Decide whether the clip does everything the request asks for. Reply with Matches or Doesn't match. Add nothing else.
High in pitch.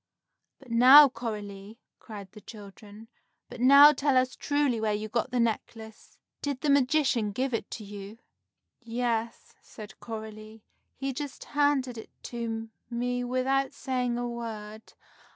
Matches